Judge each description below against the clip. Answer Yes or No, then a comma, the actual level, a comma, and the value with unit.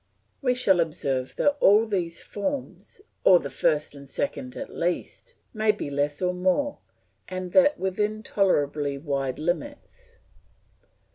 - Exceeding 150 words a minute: No, slow, 135 wpm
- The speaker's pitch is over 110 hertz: Yes, medium, 185 Hz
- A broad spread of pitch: Yes, wide, 9.0 semitones